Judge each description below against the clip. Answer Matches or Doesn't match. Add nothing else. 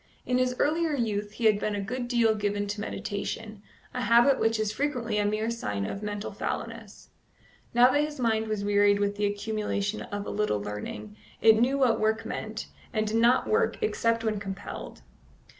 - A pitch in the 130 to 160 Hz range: Doesn't match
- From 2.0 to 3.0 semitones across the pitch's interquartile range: Matches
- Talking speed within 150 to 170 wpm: Doesn't match